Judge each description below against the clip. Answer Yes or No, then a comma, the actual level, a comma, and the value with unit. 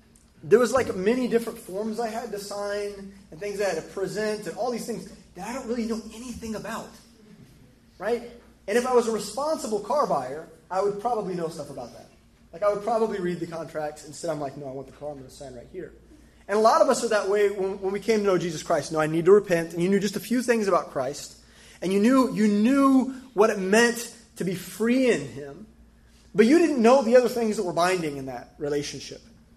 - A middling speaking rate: No, fast, 250 wpm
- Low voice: No, high, 205 Hz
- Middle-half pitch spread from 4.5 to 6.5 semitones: Yes, average, 5.1 semitones